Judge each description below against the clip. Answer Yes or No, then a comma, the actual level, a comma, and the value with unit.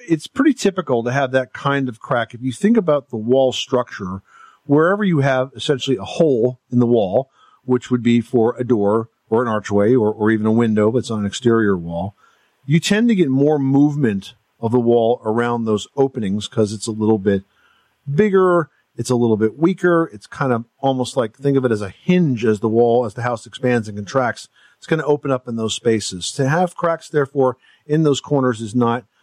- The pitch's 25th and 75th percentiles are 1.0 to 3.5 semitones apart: No, average, 4.0 semitones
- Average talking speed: No, fast, 215 wpm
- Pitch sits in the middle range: No, low, 125 Hz